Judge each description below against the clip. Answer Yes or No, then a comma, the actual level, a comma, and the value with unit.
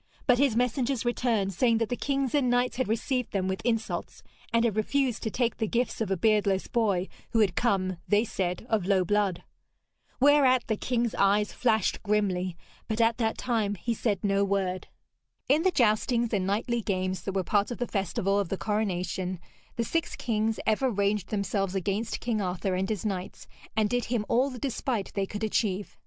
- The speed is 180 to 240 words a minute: Yes, average, 195 wpm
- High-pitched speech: Yes, high, 215 Hz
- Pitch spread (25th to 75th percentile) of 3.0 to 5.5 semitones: Yes, average, 3.5 semitones